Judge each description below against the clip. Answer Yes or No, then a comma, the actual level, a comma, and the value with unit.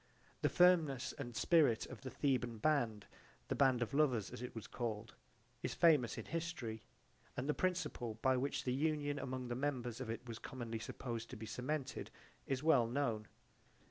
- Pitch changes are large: No, average, 3.8 semitones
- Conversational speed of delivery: Yes, average, 175 wpm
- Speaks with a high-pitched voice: No, low, 130 Hz